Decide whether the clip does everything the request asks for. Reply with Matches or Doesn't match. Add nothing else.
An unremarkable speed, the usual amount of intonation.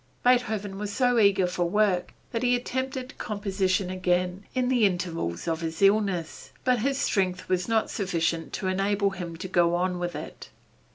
Matches